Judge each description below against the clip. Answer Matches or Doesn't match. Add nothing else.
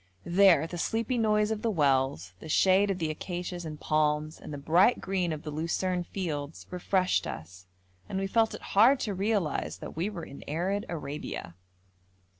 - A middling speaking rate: Matches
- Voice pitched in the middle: Matches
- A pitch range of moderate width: Matches